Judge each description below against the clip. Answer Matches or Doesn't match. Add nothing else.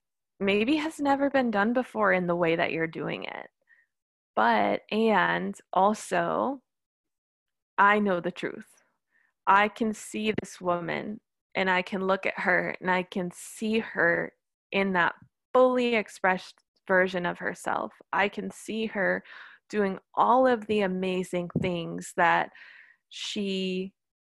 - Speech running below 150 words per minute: Matches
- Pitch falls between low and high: Doesn't match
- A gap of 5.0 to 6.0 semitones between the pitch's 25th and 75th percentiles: Doesn't match